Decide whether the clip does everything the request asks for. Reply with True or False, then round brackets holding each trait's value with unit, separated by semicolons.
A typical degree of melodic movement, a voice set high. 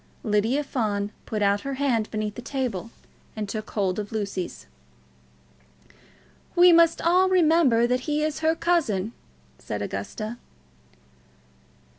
False (6.5 semitones; 235 Hz)